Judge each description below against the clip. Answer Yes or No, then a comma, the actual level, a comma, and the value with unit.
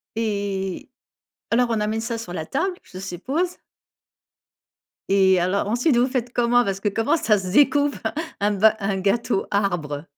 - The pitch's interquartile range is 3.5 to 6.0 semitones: Yes, average, 4.0 semitones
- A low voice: No, high, 215 Hz